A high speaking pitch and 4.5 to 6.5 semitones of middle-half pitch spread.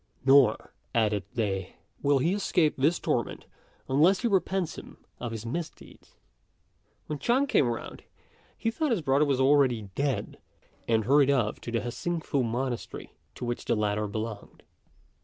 No: low, 135 Hz; wide, 5.5 semitones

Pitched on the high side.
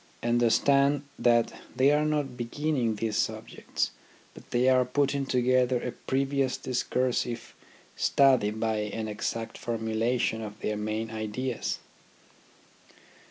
No: low, 120 Hz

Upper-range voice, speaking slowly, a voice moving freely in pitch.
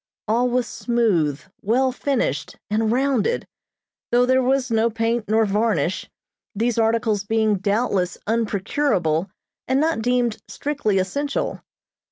No: high, 225 Hz; slow, 120 wpm; average, 3.3 semitones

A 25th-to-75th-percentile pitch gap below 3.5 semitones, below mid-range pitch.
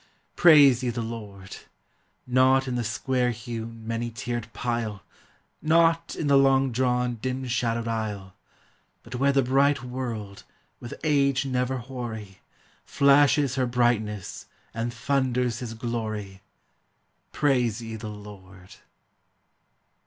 Yes: average, 2.9 semitones; low, 120 Hz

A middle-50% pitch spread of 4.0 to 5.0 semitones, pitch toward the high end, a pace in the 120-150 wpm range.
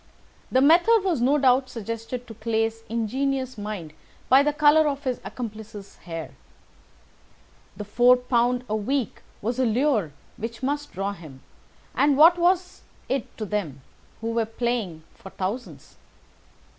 Yes: average, 4.4 semitones; high, 240 Hz; average, 145 wpm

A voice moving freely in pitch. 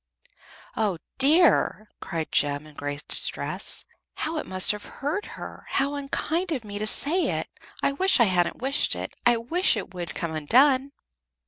Yes: wide, 8.3 semitones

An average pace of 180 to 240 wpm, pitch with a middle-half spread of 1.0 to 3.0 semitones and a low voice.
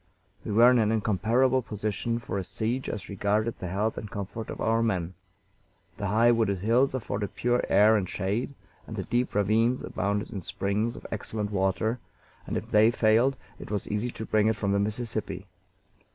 Yes: average, 185 wpm; narrow, 2.4 semitones; low, 110 Hz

